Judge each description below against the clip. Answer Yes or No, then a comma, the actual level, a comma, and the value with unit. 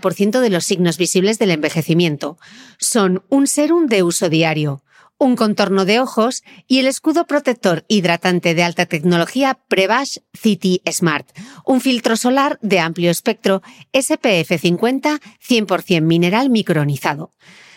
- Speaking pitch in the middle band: No, high, 195 Hz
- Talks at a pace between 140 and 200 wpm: No, average, 130 wpm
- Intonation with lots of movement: Yes, wide, 6.6 semitones